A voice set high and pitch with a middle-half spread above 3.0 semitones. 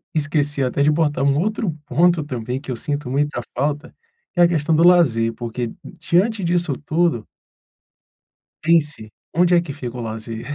No: medium, 145 Hz; average, 5.2 semitones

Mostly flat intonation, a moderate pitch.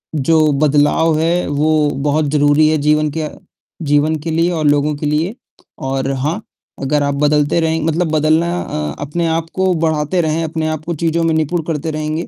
Yes: narrow, 1.8 semitones; medium, 155 Hz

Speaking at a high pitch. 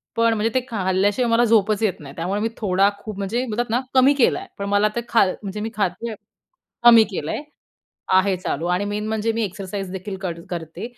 Yes: high, 205 Hz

